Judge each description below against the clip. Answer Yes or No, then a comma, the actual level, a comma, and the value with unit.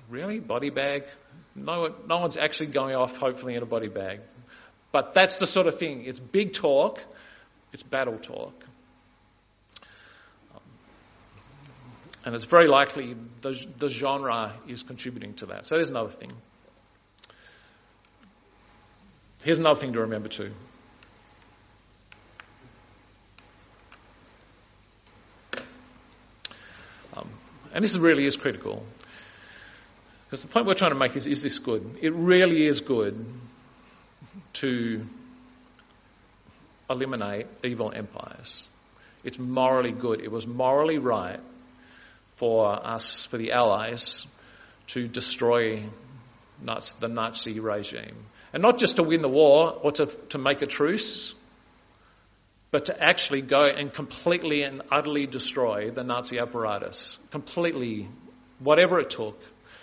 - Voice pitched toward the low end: Yes, low, 125 Hz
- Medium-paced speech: No, slow, 120 wpm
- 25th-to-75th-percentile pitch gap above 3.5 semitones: Yes, average, 4.5 semitones